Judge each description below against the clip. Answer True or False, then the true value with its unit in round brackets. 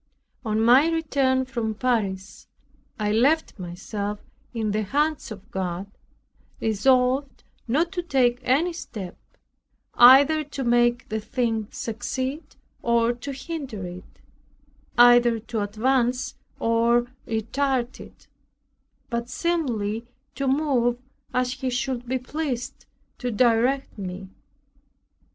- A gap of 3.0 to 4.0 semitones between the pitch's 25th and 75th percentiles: True (3.3 semitones)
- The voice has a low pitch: False (240 Hz)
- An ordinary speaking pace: False (110 wpm)